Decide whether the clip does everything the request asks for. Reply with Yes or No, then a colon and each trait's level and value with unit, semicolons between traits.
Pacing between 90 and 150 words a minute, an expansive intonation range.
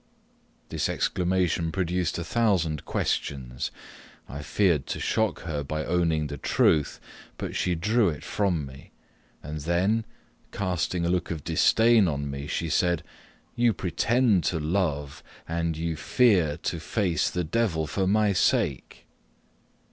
No: average, 140 wpm; average, 4.0 semitones